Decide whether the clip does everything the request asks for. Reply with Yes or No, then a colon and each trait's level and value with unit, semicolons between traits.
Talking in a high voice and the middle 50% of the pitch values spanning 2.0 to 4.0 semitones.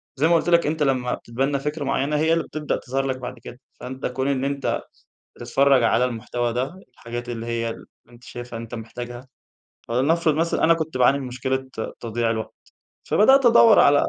No: low, 130 Hz; average, 3.6 semitones